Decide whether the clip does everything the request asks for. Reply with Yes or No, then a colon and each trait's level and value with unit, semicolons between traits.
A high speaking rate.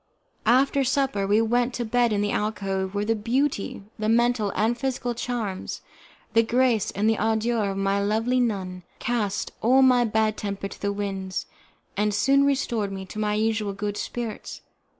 No: average, 170 wpm